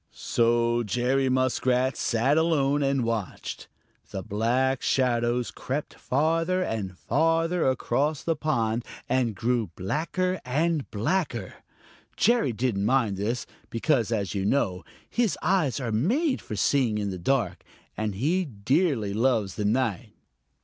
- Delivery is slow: Yes, slow, 130 wpm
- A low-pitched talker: Yes, low, 125 Hz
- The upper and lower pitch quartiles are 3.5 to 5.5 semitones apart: Yes, average, 5.1 semitones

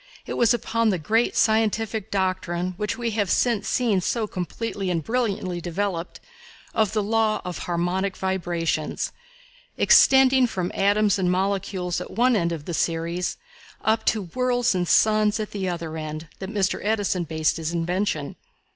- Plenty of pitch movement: No, average, 3.9 semitones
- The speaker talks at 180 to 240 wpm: No, average, 155 wpm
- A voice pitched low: No, high, 195 Hz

